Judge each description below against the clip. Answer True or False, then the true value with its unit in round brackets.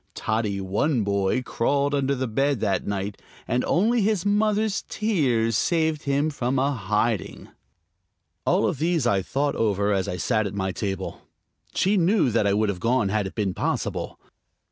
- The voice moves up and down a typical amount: False (6.7 semitones)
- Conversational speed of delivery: True (165 wpm)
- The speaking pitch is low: True (120 Hz)